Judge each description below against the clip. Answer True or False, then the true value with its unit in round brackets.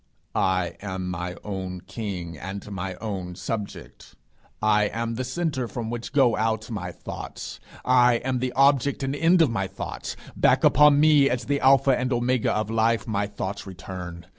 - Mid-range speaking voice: False (110 Hz)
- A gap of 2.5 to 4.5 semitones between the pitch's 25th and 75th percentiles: False (5.2 semitones)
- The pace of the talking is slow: False (170 wpm)